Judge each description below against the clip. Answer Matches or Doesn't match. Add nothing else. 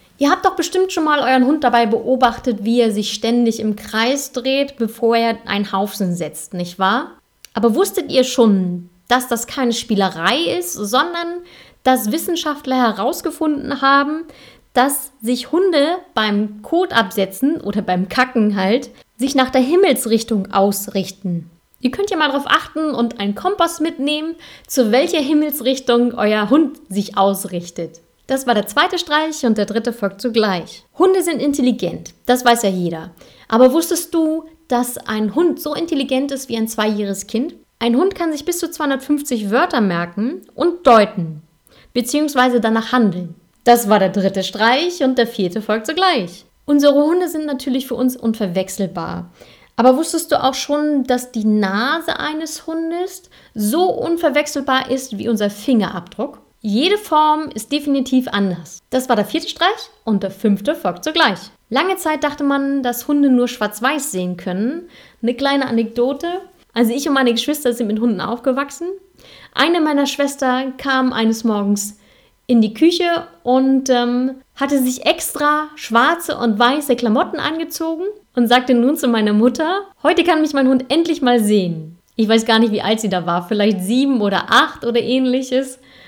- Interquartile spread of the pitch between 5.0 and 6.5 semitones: Matches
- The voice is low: Doesn't match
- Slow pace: Doesn't match